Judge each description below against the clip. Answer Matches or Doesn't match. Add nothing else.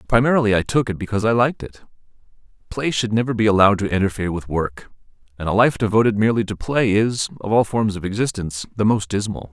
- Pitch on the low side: Matches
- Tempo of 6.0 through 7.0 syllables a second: Matches